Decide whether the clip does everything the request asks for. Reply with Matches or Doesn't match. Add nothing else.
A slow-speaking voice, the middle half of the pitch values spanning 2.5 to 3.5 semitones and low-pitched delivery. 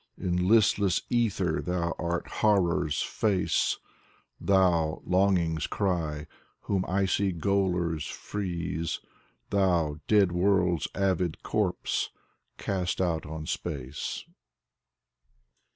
Matches